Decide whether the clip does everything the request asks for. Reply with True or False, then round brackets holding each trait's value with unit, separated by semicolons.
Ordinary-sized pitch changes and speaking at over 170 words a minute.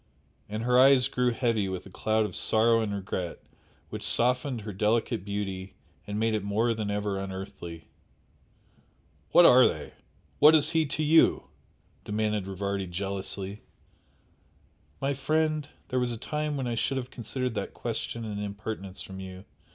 False (4.2 semitones; 160 wpm)